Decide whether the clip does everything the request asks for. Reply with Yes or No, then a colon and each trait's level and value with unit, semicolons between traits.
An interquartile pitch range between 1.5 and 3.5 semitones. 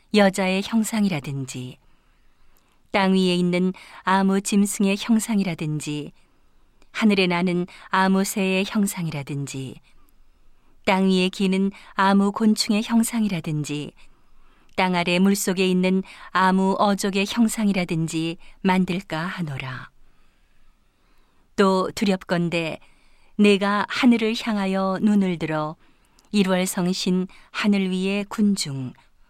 Yes: average, 2.7 semitones